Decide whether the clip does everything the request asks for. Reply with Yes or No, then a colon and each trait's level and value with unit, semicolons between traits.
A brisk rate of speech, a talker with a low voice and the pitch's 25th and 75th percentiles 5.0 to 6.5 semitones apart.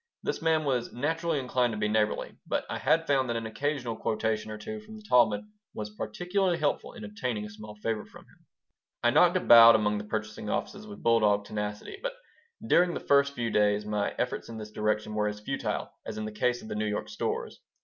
Yes: fast, 215 wpm; low, 115 Hz; average, 5.3 semitones